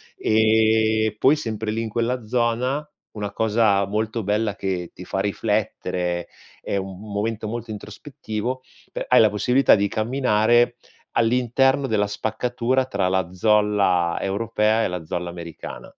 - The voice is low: Yes, low, 110 Hz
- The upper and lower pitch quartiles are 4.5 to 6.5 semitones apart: No, average, 2.7 semitones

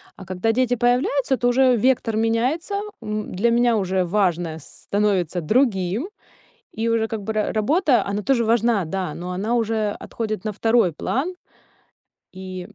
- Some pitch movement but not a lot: Yes, average, 4.3 semitones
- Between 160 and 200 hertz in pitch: No, high, 220 Hz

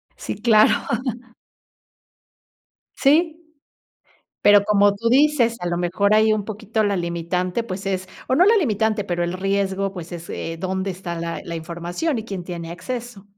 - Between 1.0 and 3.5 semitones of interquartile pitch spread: No, average, 3.9 semitones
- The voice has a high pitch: Yes, high, 195 Hz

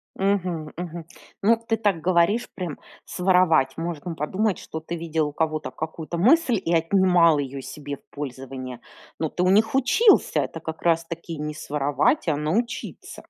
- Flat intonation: No, average, 3.6 semitones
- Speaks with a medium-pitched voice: Yes, medium, 165 Hz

